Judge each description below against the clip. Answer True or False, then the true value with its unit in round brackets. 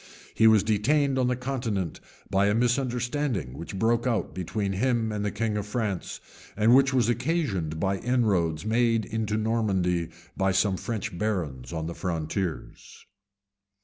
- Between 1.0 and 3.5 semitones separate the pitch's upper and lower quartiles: False (4.2 semitones)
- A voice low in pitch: True (105 Hz)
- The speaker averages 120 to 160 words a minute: True (150 wpm)